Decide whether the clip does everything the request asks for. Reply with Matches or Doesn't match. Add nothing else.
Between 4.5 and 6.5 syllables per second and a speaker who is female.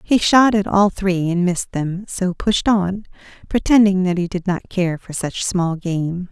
Doesn't match